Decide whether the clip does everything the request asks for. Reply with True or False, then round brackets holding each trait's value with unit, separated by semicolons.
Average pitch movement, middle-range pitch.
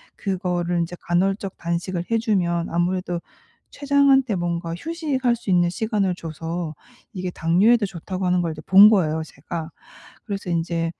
True (3.4 semitones; 180 Hz)